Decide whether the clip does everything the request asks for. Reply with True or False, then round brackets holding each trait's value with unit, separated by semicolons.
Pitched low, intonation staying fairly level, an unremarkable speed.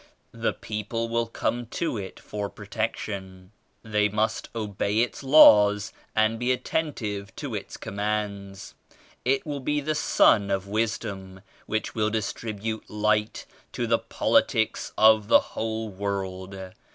False (105 Hz; 2.2 semitones; 130 wpm)